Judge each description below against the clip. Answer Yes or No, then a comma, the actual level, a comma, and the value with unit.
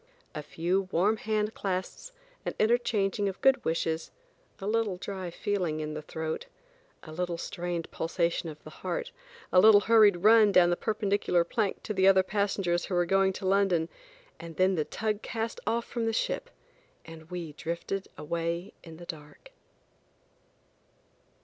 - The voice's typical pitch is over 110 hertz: Yes, medium, 185 Hz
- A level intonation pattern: No, average, 3.8 semitones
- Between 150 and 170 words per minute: Yes, average, 160 wpm